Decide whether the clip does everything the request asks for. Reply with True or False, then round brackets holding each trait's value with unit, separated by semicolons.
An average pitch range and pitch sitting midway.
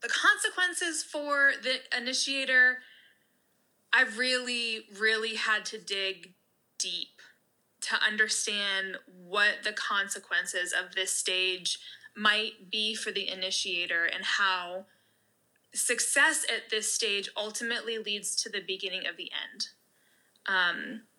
False (4.8 semitones; 215 Hz)